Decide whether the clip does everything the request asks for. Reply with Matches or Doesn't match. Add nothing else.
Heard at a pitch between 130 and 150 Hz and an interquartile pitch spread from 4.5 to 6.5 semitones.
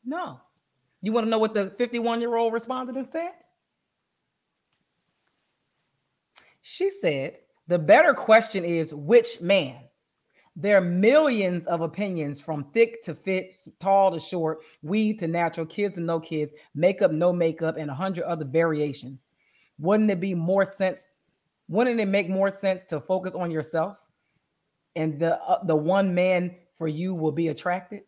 Doesn't match